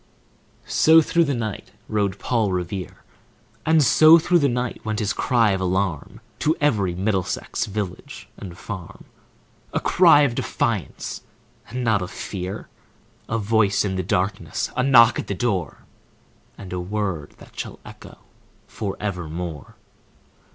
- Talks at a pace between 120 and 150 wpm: Yes, average, 140 wpm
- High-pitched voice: No, low, 105 Hz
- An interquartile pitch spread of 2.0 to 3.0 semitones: No, average, 4.6 semitones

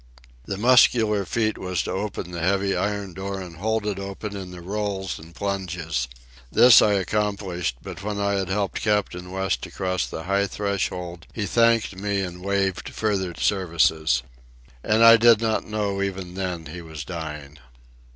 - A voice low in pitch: Yes, very low, 95 Hz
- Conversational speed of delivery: Yes, average, 165 wpm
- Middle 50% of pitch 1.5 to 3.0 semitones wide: Yes, narrow, 2.6 semitones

